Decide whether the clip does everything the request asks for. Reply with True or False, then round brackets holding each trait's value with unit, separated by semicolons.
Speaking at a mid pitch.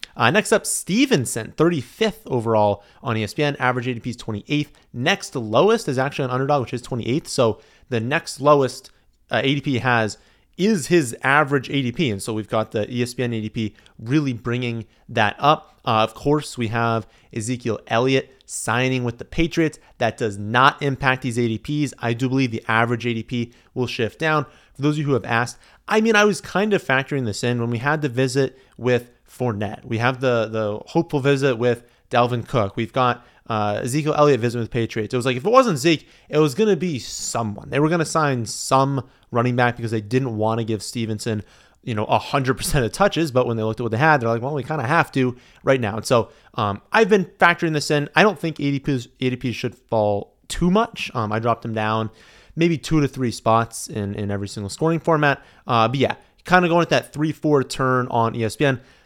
False (125 Hz)